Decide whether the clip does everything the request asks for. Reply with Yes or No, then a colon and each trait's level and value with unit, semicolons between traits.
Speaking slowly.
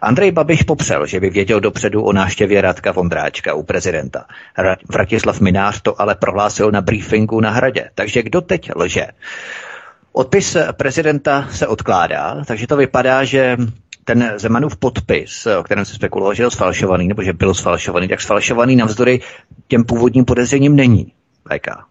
No: average, 155 wpm